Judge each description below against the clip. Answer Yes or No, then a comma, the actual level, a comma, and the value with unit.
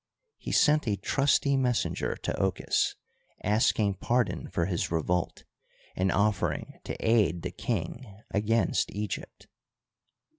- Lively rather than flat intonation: No, average, 4.0 semitones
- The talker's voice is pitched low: Yes, low, 105 Hz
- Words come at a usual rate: No, slow, 115 wpm